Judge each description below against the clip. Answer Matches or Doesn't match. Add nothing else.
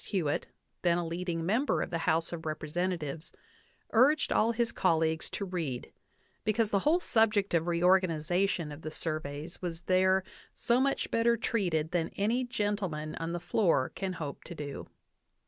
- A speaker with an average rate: Matches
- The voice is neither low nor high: Matches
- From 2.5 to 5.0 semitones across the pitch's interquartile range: Matches